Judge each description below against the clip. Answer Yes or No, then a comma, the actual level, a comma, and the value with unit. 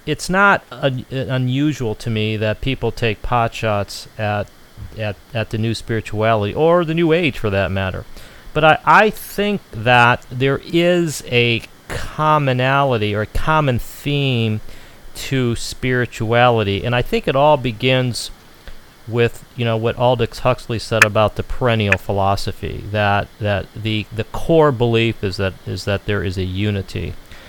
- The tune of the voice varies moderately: Yes, average, 3.8 semitones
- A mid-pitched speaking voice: No, low, 115 Hz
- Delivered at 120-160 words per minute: Yes, average, 150 wpm